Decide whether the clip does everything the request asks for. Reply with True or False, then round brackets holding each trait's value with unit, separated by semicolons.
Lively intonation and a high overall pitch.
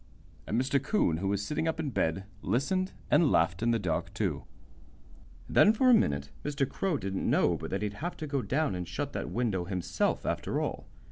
False (8.2 semitones; 120 Hz)